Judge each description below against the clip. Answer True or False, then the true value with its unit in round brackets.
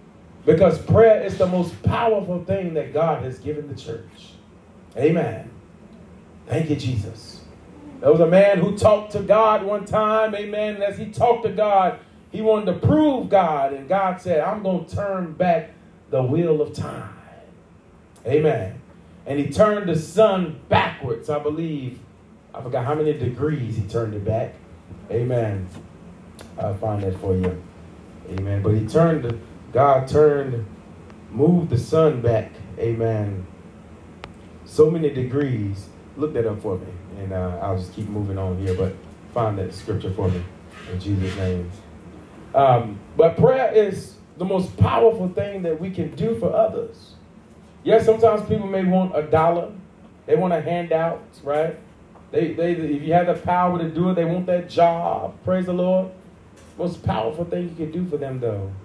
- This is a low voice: False (150 Hz)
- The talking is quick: False (170 wpm)